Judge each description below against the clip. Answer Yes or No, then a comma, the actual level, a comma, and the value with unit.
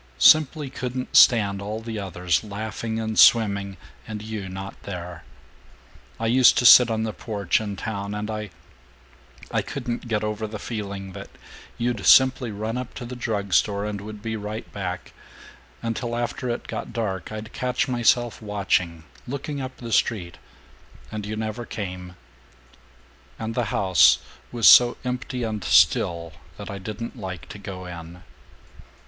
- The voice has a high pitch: No, low, 110 Hz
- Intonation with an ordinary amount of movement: Yes, average, 3.1 semitones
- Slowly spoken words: No, average, 160 wpm